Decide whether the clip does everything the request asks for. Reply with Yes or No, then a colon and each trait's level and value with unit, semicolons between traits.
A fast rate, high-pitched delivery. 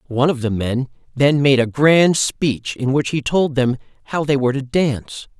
No: fast, 210 wpm; low, 135 Hz